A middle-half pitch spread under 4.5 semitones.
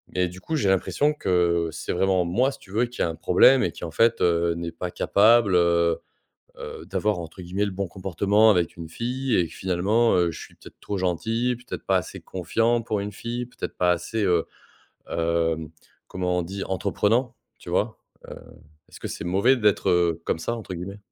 No: average, 4.8 semitones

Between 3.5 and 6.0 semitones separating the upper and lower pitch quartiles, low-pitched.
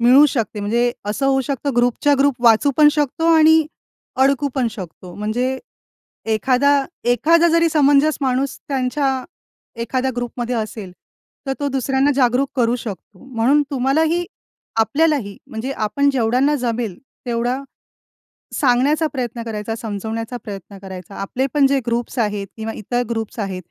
No: average, 3.8 semitones; very high, 250 Hz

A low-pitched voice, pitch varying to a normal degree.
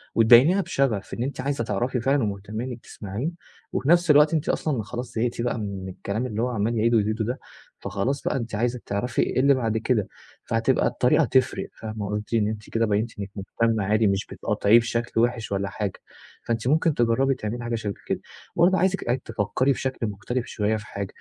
Yes: low, 115 Hz; average, 3.3 semitones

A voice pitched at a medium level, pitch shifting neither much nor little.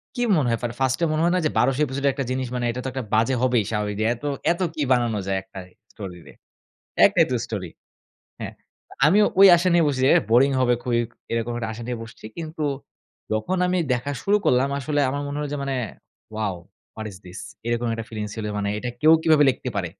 No: low, 125 Hz; average, 4.5 semitones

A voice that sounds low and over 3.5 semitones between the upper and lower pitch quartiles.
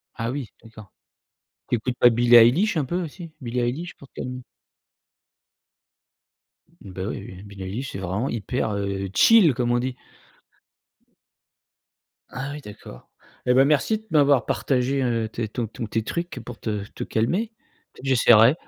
Yes: low, 120 Hz; average, 3.9 semitones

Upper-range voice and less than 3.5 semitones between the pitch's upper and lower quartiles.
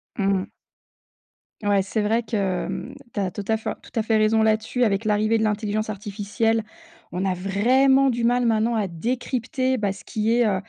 Yes: high, 215 Hz; narrow, 2.5 semitones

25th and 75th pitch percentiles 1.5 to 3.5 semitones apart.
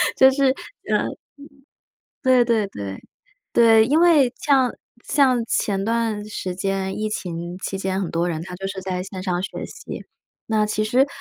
No: average, 4.5 semitones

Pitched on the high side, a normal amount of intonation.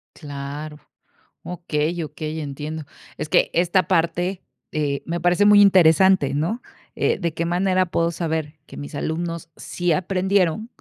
No: medium, 170 Hz; average, 3.0 semitones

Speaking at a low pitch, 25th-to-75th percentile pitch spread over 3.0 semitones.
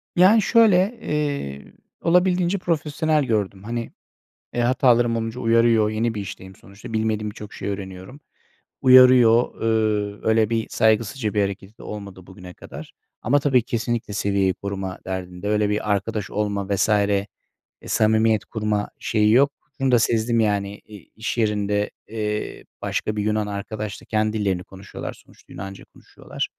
No: low, 110 Hz; average, 2.7 semitones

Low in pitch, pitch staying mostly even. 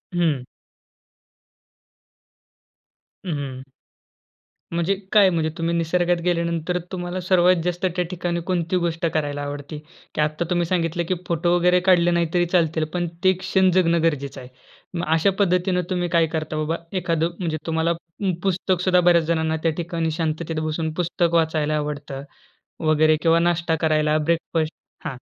No: medium, 170 Hz; narrow, 2.0 semitones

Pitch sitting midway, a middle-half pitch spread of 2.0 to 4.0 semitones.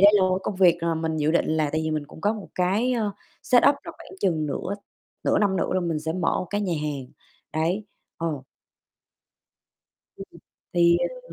Yes: medium, 175 Hz; average, 3.7 semitones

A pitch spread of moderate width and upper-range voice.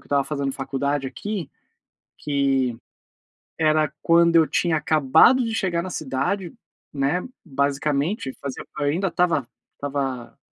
No: average, 3.6 semitones; medium, 145 Hz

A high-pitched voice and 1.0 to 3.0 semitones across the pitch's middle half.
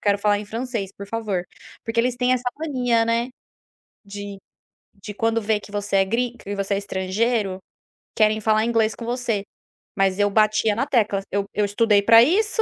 Yes: high, 215 Hz; narrow, 2.6 semitones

